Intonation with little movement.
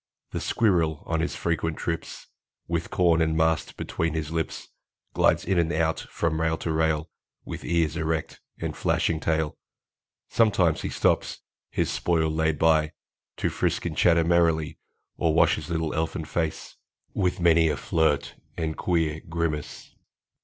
Yes: narrow, 1.0 semitones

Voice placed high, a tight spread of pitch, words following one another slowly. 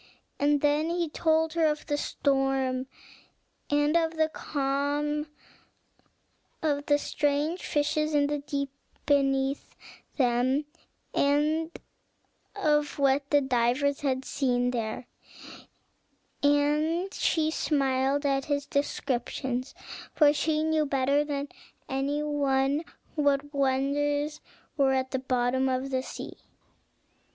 Yes: very high, 285 Hz; narrow, 1.8 semitones; slow, 105 wpm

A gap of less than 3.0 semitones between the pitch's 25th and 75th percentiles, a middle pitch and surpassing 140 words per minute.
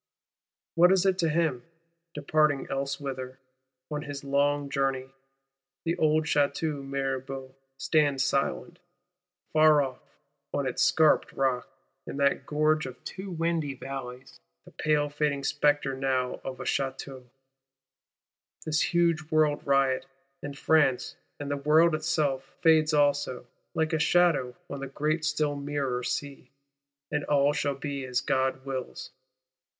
No: narrow, 2.4 semitones; medium, 145 Hz; slow, 135 wpm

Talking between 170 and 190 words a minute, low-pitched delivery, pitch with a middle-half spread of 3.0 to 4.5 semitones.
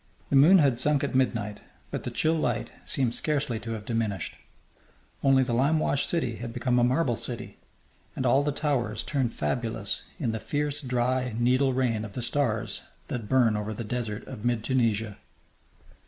Yes: average, 175 wpm; low, 125 Hz; average, 3.3 semitones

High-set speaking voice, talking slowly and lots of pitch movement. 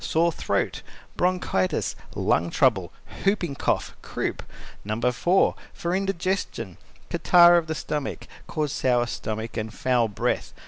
No: medium, 140 Hz; slow, 125 wpm; wide, 7.6 semitones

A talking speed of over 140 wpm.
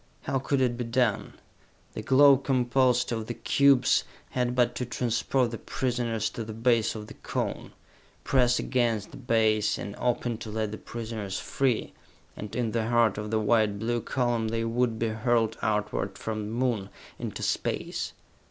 Yes: average, 170 wpm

